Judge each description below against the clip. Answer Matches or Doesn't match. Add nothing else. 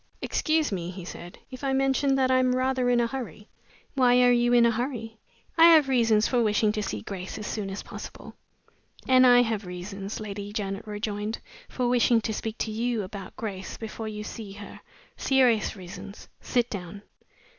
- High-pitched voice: Matches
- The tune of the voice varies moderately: Matches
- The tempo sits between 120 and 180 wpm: Doesn't match